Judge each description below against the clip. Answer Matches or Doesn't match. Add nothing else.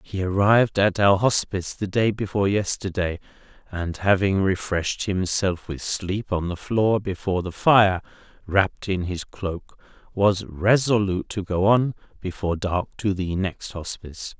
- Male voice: Matches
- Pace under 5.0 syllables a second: Matches